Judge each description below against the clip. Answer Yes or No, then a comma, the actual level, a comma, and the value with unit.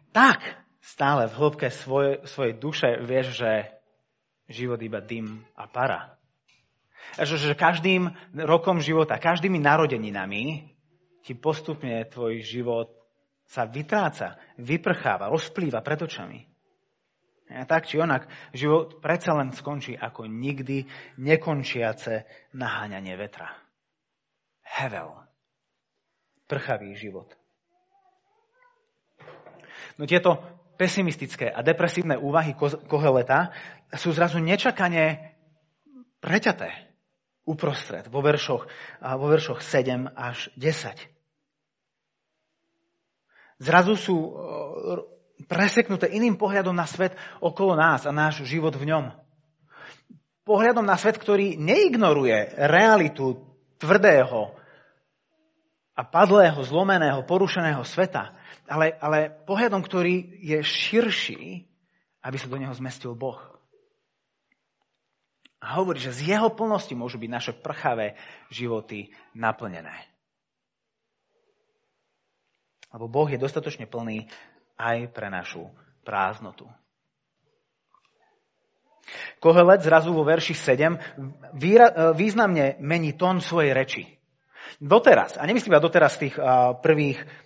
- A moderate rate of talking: No, slow, 100 wpm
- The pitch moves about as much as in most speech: No, wide, 5.7 semitones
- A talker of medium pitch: Yes, medium, 155 Hz